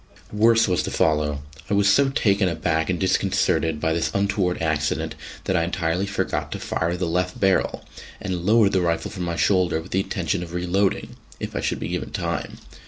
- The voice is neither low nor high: No, very low, 90 Hz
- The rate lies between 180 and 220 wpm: Yes, average, 195 wpm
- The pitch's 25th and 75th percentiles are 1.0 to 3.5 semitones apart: Yes, average, 3.1 semitones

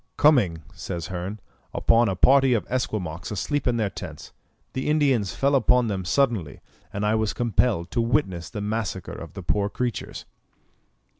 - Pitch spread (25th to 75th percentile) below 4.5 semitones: No, average, 5.0 semitones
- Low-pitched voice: Yes, low, 110 Hz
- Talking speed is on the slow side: No, average, 160 wpm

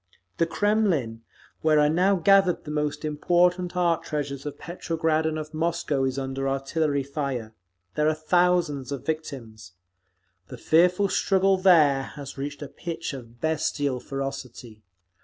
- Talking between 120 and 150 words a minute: Yes, average, 140 wpm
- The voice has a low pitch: No, medium, 150 Hz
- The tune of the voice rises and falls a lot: No, average, 3.9 semitones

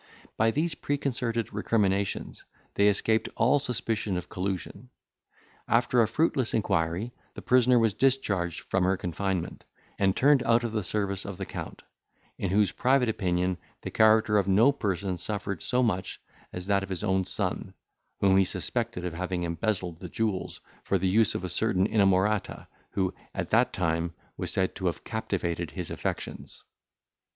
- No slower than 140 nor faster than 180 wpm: Yes, average, 160 wpm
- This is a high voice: No, low, 100 Hz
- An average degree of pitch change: Yes, average, 3.7 semitones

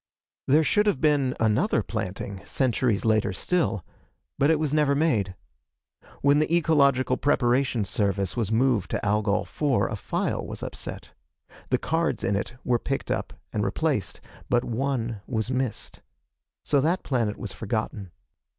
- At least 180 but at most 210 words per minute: No, average, 150 wpm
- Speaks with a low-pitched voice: Yes, low, 125 Hz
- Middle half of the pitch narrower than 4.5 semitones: No, average, 5.0 semitones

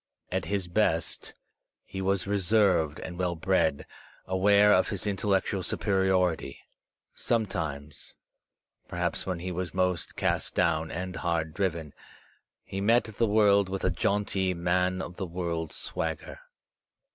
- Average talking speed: No, slow, 130 wpm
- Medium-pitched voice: No, very low, 95 Hz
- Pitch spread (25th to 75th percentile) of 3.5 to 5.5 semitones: No, average, 2.7 semitones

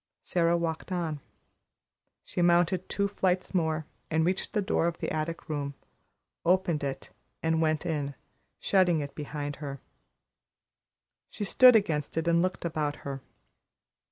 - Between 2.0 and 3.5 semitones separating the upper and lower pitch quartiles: Yes, average, 3.1 semitones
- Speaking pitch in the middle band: Yes, medium, 165 Hz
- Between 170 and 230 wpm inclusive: No, average, 140 wpm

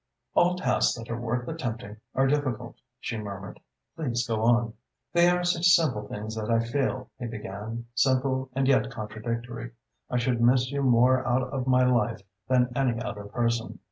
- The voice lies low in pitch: Yes, low, 120 Hz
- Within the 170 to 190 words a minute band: Yes, average, 175 wpm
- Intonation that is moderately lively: No, narrow, 2.3 semitones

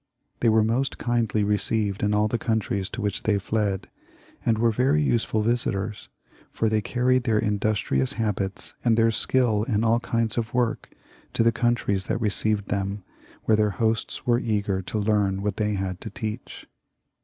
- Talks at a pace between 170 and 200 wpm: Yes, average, 175 wpm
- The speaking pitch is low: Yes, low, 110 Hz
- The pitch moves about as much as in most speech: No, narrow, 2.2 semitones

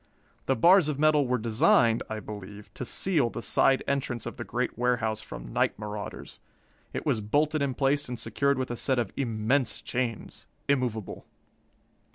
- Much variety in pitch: No, average, 4.2 semitones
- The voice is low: Yes, low, 125 Hz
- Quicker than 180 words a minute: No, average, 170 wpm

